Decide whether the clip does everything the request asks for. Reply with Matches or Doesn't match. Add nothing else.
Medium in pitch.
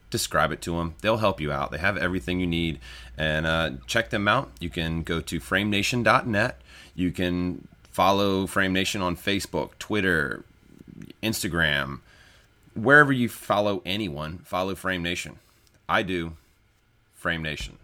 Doesn't match